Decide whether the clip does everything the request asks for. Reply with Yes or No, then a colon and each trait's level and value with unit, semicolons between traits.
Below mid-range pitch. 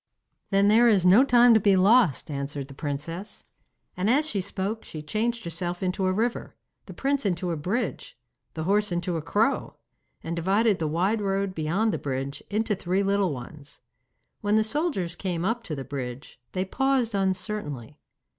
No: high, 190 Hz